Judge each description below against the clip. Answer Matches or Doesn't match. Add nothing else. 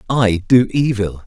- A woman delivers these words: Doesn't match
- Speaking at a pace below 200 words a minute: Matches